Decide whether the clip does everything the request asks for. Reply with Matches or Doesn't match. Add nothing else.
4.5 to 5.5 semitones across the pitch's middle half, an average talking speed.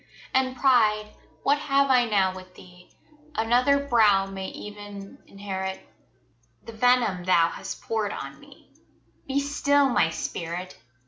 Doesn't match